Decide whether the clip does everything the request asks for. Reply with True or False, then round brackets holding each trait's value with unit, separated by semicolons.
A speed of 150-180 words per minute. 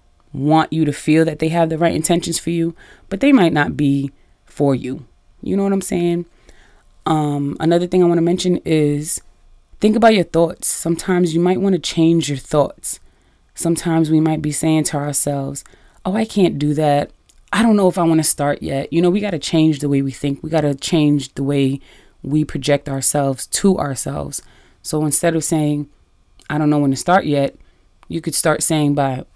False (200 wpm)